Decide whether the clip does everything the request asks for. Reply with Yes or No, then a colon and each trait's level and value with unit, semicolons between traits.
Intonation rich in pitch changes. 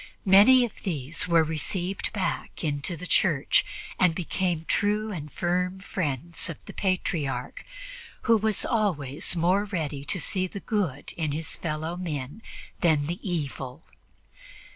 No: average, 4.0 semitones